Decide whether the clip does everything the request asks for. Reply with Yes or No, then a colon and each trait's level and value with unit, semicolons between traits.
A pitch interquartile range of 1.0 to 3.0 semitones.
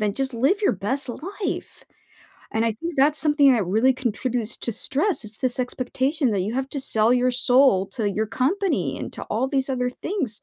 No: average, 3.9 semitones